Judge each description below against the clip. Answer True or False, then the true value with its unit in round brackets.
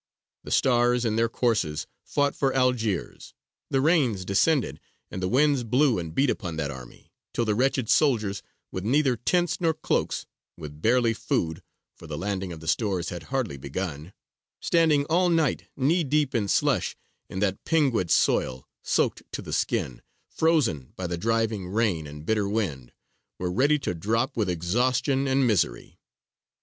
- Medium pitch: False (115 Hz)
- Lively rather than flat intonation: True (7.1 semitones)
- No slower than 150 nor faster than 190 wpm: True (160 wpm)